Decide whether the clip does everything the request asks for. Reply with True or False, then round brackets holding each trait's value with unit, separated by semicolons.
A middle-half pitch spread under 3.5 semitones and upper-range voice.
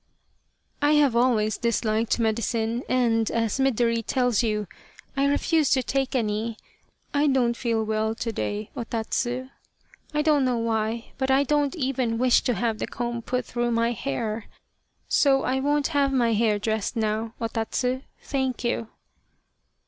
True (2.9 semitones; 235 Hz)